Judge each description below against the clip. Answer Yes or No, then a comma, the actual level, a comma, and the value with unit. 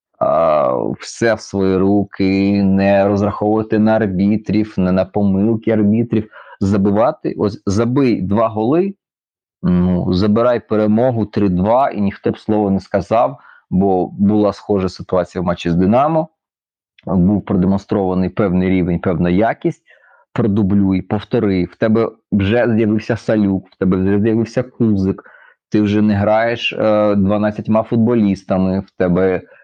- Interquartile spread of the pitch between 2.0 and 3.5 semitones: Yes, narrow, 2.6 semitones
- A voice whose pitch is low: Yes, low, 100 Hz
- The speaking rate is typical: Yes, average, 125 wpm